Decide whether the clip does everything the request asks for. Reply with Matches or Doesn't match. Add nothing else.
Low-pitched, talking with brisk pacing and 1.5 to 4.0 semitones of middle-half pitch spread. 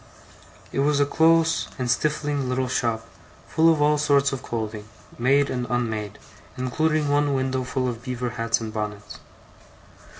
Doesn't match